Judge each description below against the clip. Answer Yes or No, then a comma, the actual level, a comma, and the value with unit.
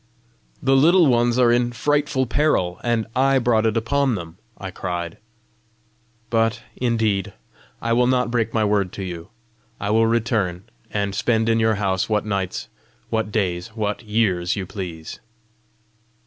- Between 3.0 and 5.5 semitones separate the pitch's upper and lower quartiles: Yes, average, 3.5 semitones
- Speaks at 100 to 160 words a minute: Yes, average, 155 wpm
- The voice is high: No, low, 110 Hz